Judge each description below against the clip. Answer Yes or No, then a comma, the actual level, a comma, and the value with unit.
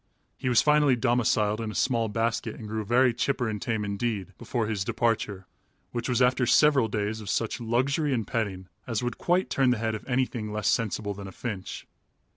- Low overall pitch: Yes, low, 115 Hz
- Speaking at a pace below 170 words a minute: No, average, 200 wpm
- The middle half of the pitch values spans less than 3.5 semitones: Yes, average, 2.8 semitones